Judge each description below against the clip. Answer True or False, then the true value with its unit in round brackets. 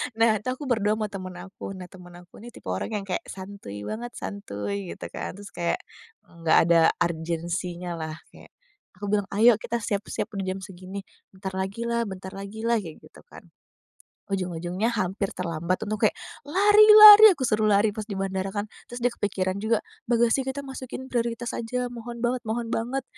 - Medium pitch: False (205 Hz)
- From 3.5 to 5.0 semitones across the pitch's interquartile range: True (4.1 semitones)